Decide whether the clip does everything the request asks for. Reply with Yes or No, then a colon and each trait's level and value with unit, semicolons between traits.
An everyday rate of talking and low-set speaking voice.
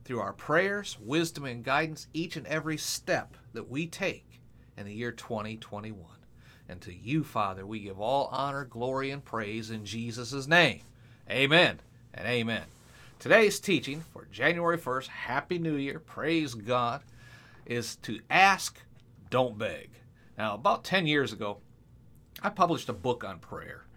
Yes: average, 150 wpm; low, 125 Hz